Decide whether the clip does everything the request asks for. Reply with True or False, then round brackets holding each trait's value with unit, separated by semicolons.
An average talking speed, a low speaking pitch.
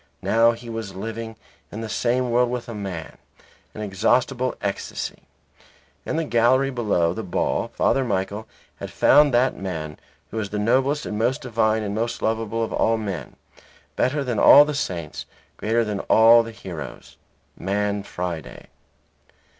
True (155 wpm; 110 Hz)